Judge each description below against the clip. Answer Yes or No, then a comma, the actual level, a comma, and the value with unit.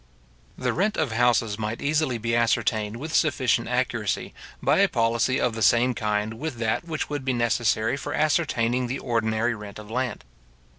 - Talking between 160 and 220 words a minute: Yes, average, 170 wpm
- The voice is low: Yes, low, 120 Hz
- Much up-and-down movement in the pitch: No, average, 2.7 semitones